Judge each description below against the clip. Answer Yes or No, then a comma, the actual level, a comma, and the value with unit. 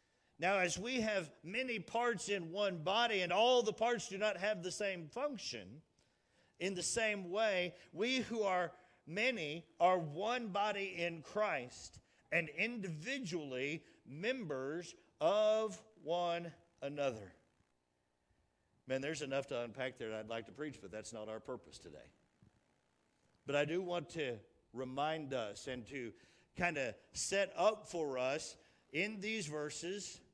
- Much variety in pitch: Yes, wide, 7.4 semitones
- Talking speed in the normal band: Yes, average, 145 wpm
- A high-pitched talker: No, medium, 175 Hz